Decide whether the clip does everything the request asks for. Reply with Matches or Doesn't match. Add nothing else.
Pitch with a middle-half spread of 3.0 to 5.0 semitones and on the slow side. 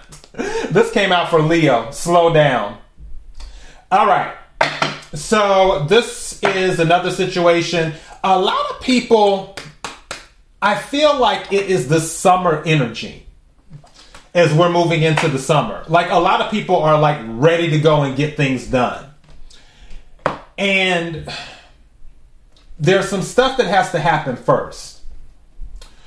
Matches